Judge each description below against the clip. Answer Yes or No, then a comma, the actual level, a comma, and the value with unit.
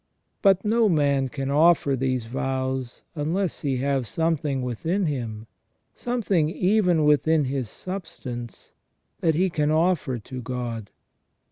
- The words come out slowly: Yes, slow, 125 wpm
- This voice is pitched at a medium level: Yes, medium, 145 Hz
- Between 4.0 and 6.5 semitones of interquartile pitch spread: Yes, average, 4.9 semitones